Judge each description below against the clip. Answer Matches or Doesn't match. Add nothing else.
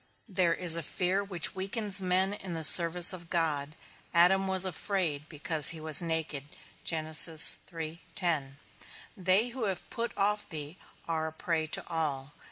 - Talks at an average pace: Matches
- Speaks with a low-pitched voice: Doesn't match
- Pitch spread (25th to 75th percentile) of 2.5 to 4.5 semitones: Matches